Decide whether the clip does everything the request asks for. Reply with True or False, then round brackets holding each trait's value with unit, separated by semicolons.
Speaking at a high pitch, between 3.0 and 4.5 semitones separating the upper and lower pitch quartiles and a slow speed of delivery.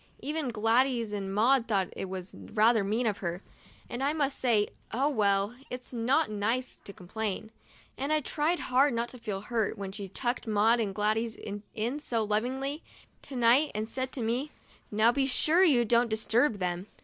False (230 Hz; 3.8 semitones; 195 wpm)